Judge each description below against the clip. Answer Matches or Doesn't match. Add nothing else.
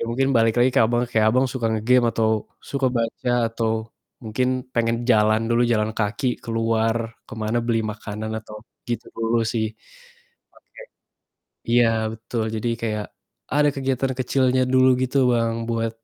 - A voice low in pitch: Matches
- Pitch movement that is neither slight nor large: Doesn't match